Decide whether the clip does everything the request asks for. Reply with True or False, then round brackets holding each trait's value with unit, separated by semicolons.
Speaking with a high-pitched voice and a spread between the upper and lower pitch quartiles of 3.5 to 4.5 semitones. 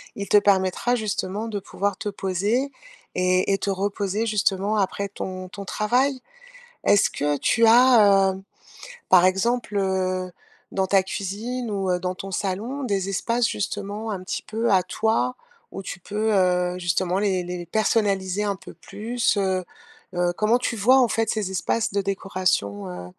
False (200 Hz; 2.7 semitones)